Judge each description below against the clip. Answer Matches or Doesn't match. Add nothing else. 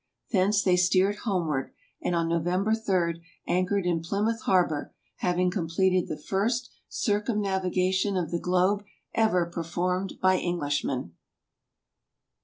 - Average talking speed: Doesn't match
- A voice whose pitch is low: Doesn't match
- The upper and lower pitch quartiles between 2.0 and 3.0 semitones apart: Matches